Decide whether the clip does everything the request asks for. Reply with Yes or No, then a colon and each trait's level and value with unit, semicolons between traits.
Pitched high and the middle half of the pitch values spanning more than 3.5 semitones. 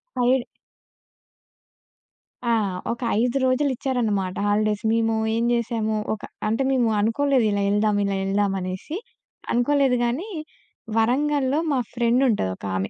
Yes: high, 230 Hz; average, 3.9 semitones